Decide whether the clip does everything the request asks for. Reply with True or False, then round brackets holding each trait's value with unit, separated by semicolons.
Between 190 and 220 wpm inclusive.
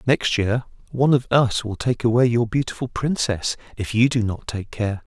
True (200 wpm)